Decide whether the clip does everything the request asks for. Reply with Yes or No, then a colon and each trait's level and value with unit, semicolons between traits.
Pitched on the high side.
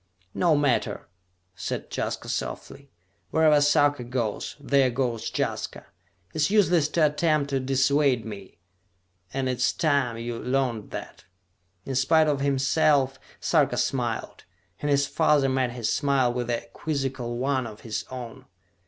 No: low, 135 Hz